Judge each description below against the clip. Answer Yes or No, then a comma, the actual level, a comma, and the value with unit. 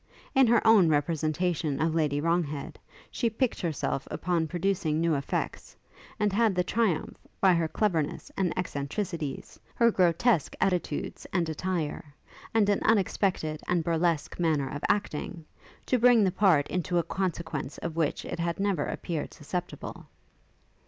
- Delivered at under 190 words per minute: Yes, average, 145 wpm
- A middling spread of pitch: Yes, average, 3.9 semitones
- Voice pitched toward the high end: No, medium, 170 Hz